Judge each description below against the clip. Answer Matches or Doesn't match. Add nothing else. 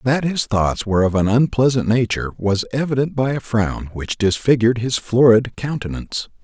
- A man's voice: Matches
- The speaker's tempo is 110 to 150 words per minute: Doesn't match